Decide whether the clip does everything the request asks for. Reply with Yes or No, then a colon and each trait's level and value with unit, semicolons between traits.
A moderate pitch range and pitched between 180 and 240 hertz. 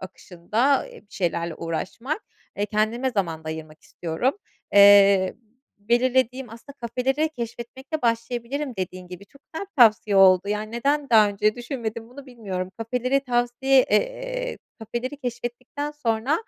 Yes: average, 4.7 semitones; high, 235 Hz